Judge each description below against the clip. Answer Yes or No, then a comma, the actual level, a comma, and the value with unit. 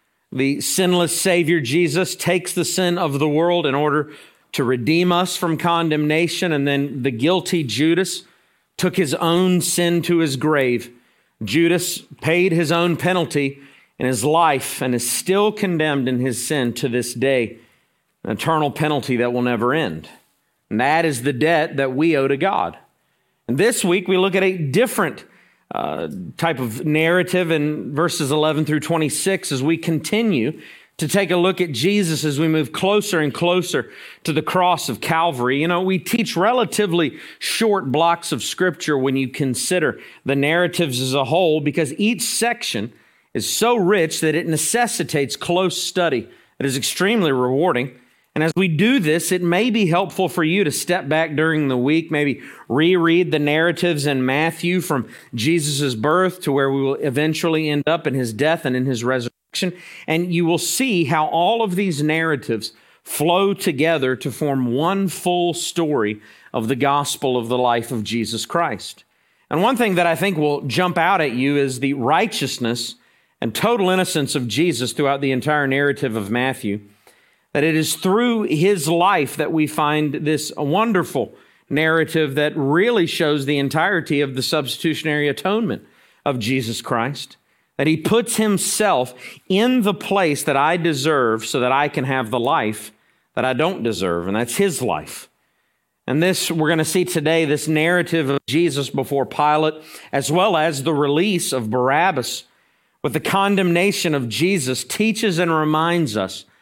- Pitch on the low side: No, medium, 155 Hz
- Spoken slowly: No, average, 170 wpm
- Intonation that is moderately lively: Yes, average, 4.3 semitones